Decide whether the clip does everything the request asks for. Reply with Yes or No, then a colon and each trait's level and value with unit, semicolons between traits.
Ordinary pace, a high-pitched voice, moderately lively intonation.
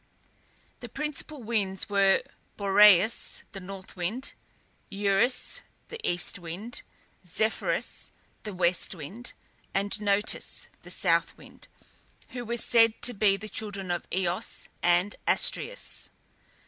No: slow, 115 wpm; high, 200 Hz; average, 3.3 semitones